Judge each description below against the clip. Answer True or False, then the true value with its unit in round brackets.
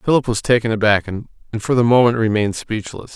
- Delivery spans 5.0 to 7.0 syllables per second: True (6.1 syllables/s)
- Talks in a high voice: False (115 Hz)